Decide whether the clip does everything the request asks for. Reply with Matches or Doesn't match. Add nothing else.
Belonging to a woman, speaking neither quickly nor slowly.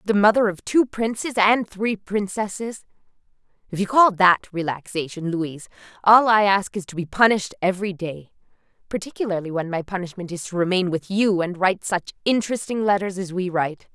Matches